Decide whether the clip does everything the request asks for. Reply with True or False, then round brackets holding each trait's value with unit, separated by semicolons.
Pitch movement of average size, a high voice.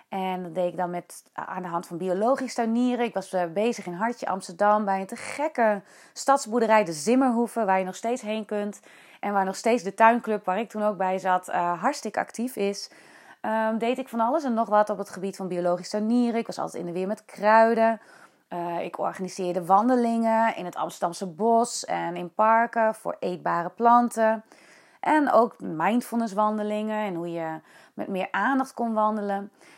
True (3.8 semitones; 215 Hz)